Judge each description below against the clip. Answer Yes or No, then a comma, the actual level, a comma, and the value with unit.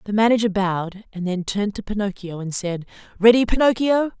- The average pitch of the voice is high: Yes, high, 205 Hz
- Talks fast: No, average, 170 wpm